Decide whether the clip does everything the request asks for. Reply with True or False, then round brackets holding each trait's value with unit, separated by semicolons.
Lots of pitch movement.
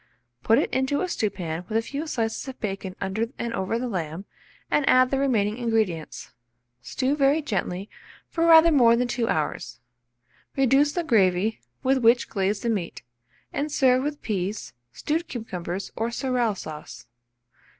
True (5.7 semitones)